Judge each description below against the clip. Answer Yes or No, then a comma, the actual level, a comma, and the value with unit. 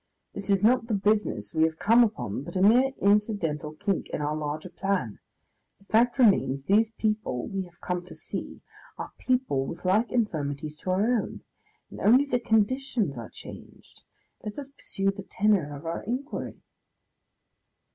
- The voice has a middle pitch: No, high, 200 Hz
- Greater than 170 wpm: No, average, 165 wpm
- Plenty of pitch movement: Yes, wide, 6.2 semitones